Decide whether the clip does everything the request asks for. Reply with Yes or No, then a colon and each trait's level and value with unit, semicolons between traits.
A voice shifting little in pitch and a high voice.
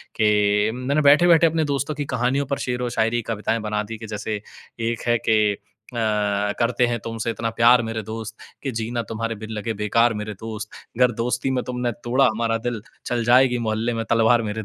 No: narrow, 2.1 semitones; low, 115 Hz